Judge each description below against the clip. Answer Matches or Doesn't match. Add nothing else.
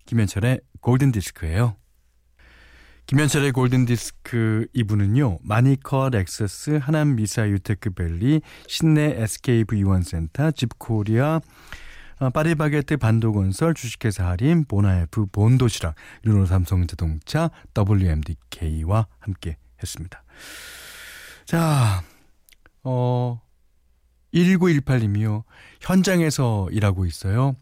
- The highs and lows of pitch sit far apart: Matches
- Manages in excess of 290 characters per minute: Doesn't match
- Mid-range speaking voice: Doesn't match